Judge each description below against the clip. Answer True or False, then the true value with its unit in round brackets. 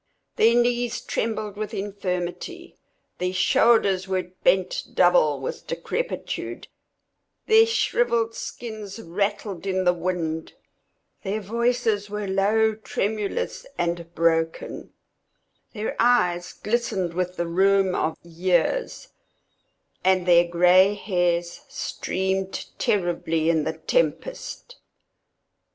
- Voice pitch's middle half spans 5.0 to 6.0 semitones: False (3.9 semitones)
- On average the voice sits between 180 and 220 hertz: True (190 Hz)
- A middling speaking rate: False (100 wpm)